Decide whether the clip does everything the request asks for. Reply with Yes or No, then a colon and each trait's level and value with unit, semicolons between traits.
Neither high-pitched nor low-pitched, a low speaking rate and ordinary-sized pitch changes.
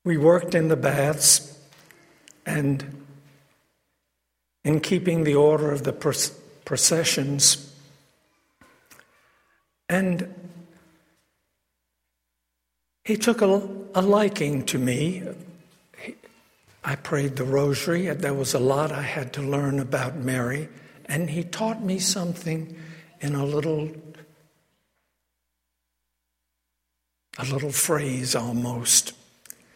Yes: medium, 145 Hz; slow, 100 wpm; average, 4.8 semitones